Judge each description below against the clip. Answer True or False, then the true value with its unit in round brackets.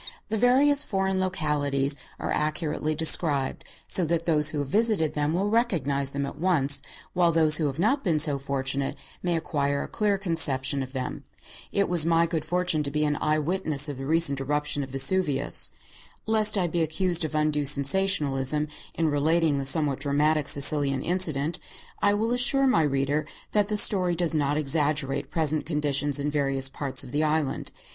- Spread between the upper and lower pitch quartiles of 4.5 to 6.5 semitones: False (3.8 semitones)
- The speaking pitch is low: False (155 Hz)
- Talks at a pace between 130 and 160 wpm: False (180 wpm)